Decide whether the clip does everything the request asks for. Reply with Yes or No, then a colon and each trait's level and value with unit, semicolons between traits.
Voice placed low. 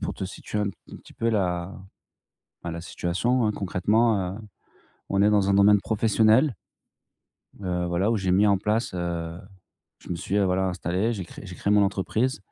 Yes: low, 100 Hz